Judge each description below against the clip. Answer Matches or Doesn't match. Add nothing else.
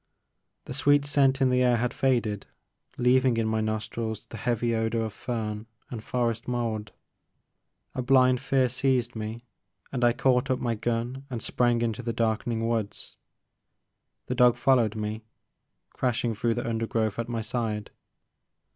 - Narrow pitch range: Matches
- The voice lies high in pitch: Doesn't match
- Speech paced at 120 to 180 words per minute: Matches